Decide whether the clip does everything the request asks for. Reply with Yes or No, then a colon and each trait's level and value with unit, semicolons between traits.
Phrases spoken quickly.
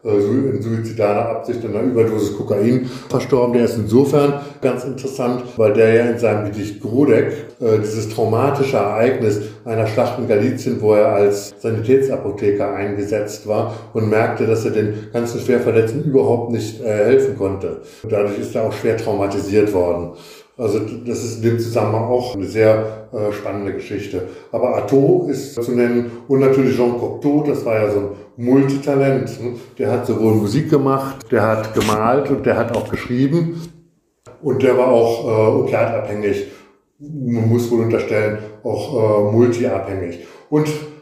No: average, 160 wpm